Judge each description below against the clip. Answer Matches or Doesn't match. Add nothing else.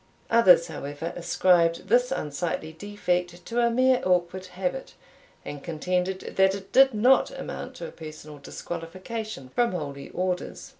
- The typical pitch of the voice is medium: Matches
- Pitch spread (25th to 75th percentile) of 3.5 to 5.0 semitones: Matches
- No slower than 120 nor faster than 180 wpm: Matches